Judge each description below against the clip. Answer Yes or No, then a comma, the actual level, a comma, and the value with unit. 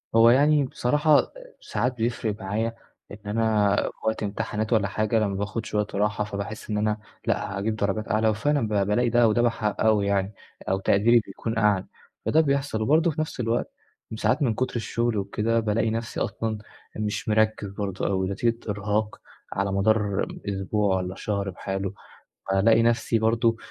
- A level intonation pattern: Yes, narrow, 2.3 semitones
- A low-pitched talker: Yes, low, 110 Hz